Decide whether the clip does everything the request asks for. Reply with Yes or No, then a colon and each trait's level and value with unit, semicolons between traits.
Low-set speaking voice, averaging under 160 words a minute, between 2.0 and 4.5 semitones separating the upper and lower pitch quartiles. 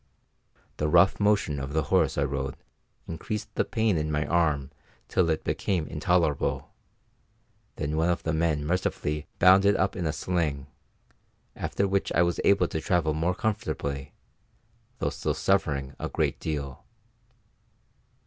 Yes: very low, 80 Hz; average, 150 wpm; average, 3.7 semitones